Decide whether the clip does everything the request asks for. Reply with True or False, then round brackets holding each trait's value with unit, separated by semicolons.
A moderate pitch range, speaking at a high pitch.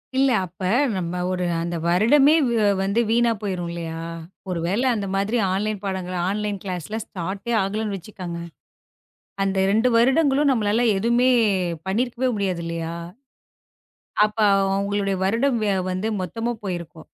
True (4.1 semitones; 200 Hz)